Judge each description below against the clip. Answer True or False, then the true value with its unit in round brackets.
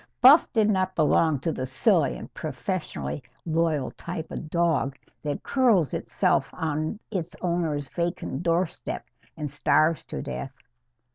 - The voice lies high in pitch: False (160 Hz)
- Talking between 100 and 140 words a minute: True (135 wpm)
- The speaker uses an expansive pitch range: False (3.3 semitones)